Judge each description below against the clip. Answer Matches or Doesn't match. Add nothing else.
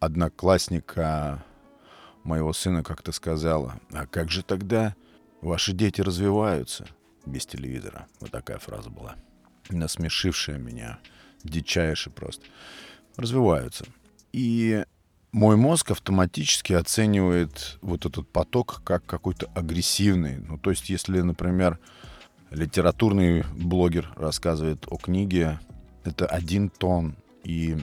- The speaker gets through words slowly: Matches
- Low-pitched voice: Matches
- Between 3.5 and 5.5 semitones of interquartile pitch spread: Doesn't match